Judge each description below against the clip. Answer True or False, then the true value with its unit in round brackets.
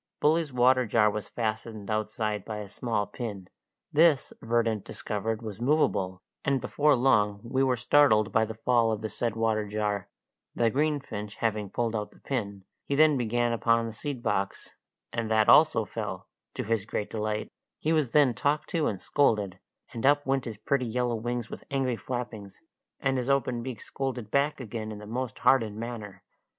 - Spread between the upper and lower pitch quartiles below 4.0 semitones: True (3.5 semitones)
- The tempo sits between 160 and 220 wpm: True (180 wpm)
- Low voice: True (115 Hz)